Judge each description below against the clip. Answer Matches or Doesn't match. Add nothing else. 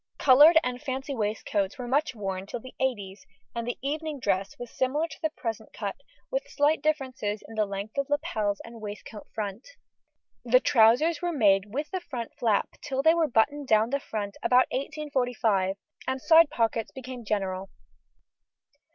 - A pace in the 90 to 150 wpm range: Doesn't match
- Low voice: Doesn't match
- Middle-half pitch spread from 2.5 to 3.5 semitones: Doesn't match